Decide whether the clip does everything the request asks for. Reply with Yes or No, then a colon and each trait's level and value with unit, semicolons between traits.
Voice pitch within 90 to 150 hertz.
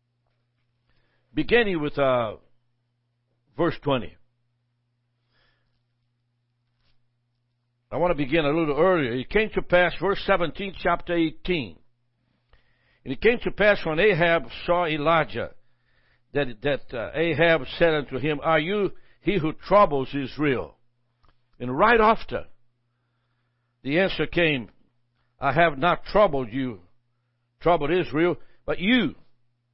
Yes: low, 135 Hz